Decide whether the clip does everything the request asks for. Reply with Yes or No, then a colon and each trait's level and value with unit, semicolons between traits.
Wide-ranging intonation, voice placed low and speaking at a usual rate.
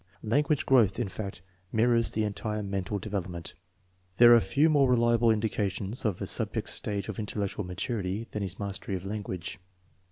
No: average, 3.1 semitones; low, 105 Hz; average, 165 wpm